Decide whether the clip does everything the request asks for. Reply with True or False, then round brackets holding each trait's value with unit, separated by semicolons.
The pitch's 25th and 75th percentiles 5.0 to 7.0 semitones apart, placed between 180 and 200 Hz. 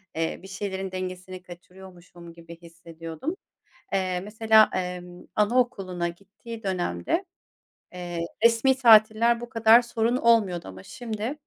False (4.5 semitones; 190 Hz)